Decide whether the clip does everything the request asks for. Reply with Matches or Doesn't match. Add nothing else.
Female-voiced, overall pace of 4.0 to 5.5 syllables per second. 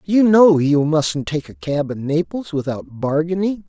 Doesn't match